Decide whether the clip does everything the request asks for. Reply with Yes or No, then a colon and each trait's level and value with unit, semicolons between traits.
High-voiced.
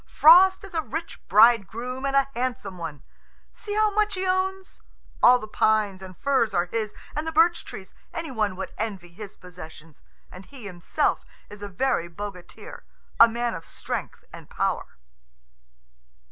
Yes: high, 225 Hz